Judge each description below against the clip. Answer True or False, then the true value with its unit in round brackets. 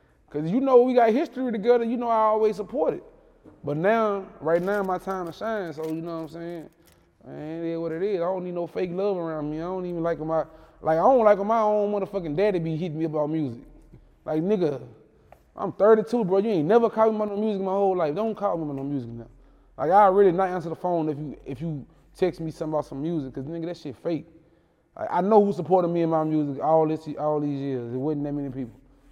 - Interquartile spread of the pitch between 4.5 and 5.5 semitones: True (5.0 semitones)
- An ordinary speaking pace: False (250 wpm)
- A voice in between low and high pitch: True (170 Hz)